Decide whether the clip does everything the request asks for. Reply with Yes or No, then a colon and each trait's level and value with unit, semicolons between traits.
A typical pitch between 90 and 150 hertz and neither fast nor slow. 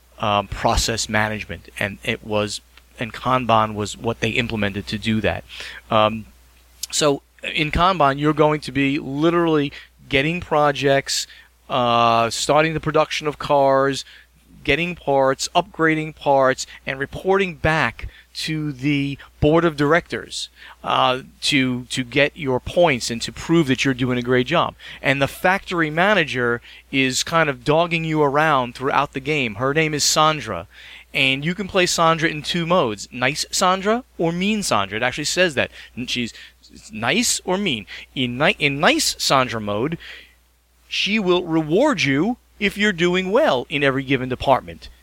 Yes: medium, 140 Hz; average, 155 wpm